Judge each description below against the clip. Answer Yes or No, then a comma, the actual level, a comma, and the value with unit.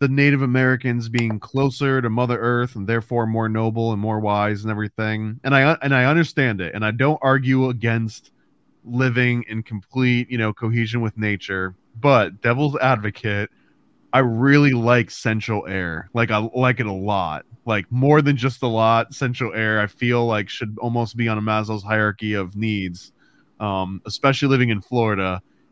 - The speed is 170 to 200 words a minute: Yes, average, 175 wpm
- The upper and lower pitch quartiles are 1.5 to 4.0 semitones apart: Yes, average, 3.1 semitones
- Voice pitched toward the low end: Yes, low, 115 Hz